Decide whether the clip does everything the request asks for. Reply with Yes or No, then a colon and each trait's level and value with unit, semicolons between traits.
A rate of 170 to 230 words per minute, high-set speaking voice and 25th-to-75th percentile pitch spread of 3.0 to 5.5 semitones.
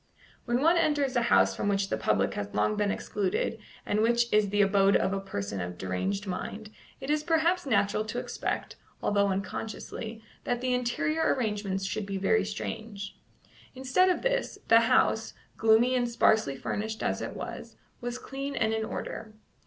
Yes: average, 175 wpm; high, 220 Hz; average, 4.1 semitones